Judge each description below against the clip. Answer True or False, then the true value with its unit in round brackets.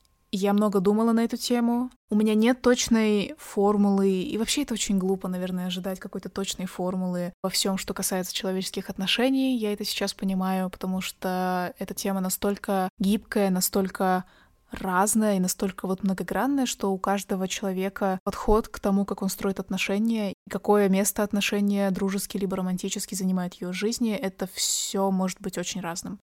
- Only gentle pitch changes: True (1.9 semitones)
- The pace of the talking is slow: False (160 wpm)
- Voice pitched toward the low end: False (200 Hz)